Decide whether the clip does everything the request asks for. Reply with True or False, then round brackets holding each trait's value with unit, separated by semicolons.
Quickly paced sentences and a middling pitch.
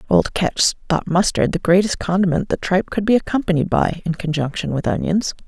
False (185 wpm; 180 Hz)